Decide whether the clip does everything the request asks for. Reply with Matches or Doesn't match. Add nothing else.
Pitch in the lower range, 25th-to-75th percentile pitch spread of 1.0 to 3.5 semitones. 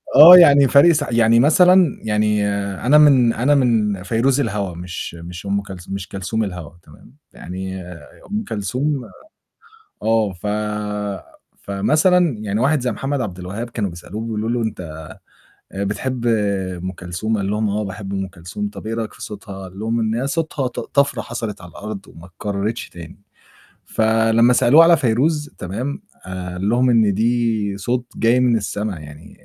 Doesn't match